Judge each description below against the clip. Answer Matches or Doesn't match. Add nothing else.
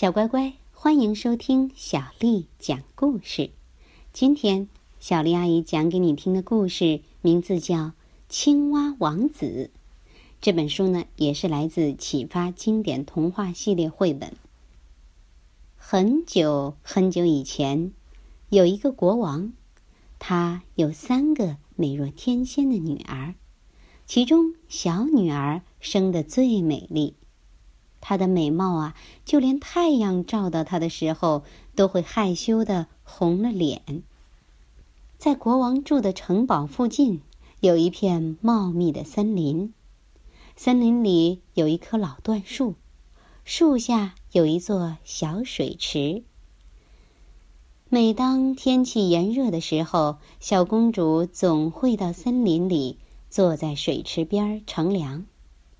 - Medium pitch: Matches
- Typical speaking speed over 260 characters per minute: Doesn't match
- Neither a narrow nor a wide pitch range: Doesn't match